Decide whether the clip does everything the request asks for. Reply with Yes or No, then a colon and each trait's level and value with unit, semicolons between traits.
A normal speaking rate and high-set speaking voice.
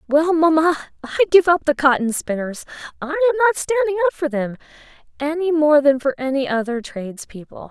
Yes: average, 180 wpm; very high, 300 Hz